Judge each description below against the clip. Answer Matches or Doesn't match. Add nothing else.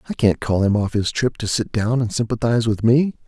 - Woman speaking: Doesn't match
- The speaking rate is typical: Doesn't match